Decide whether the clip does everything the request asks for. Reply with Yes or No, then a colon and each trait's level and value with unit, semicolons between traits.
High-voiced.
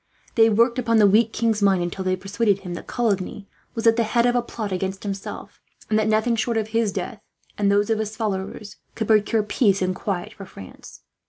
Yes: high, 210 Hz